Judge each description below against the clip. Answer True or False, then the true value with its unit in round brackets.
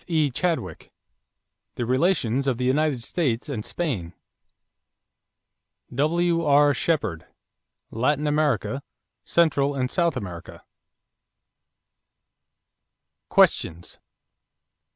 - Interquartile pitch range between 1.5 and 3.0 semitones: False (4.8 semitones)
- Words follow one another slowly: True (80 wpm)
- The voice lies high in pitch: False (140 Hz)